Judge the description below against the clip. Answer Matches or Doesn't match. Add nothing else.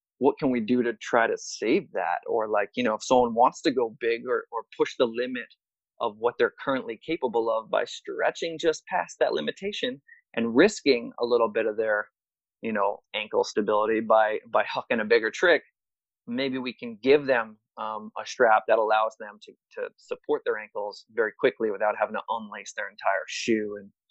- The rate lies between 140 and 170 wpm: Doesn't match